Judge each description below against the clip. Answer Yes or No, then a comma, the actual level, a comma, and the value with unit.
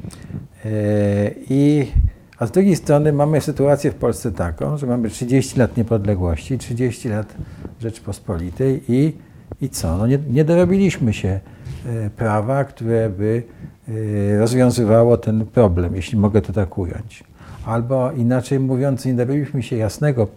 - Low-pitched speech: Yes, low, 115 Hz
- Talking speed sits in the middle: Yes, average, 130 wpm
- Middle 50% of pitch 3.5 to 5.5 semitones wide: Yes, average, 4.2 semitones